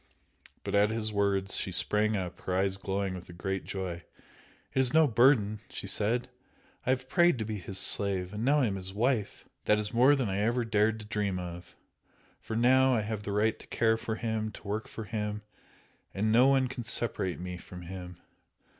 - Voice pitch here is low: Yes, low, 105 Hz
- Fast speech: Yes, fast, 210 wpm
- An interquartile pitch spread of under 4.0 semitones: Yes, average, 3.4 semitones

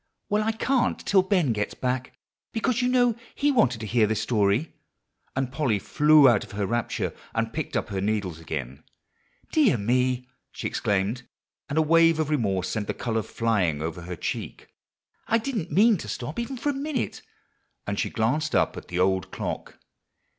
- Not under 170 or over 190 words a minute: Yes, average, 180 wpm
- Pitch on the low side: Yes, low, 125 Hz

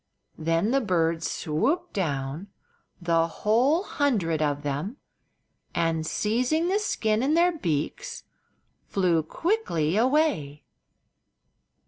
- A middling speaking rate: No, slow, 90 wpm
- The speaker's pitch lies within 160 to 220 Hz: Yes, high, 190 Hz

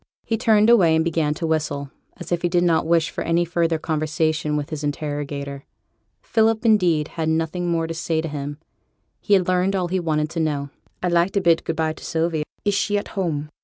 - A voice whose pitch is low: No, medium, 165 Hz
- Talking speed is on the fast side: Yes, fast, 215 wpm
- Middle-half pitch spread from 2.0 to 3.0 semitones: Yes, narrow, 2.6 semitones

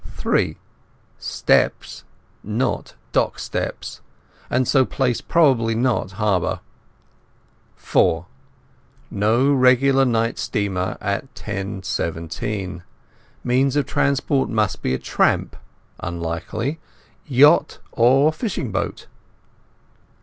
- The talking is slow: Yes, slow, 85 wpm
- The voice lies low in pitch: Yes, low, 115 Hz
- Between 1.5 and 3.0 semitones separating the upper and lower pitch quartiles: No, wide, 5.4 semitones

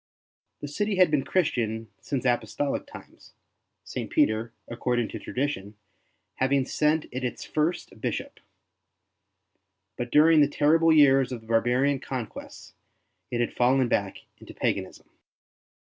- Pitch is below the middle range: Yes, low, 130 Hz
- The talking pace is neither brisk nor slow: No, slow, 130 wpm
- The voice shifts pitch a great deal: No, average, 3.8 semitones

